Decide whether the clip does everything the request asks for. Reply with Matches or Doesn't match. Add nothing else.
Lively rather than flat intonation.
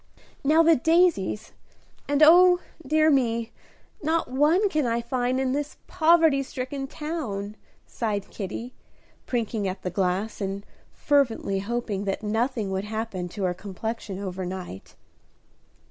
Matches